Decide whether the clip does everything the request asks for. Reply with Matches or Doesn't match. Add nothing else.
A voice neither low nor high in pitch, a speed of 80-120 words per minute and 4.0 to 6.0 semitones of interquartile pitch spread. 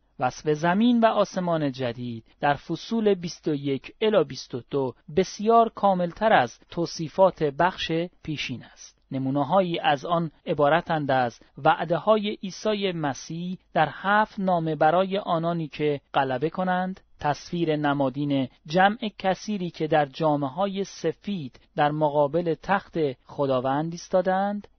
Matches